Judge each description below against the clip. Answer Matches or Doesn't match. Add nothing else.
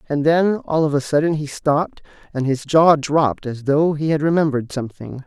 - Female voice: Doesn't match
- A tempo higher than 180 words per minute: Matches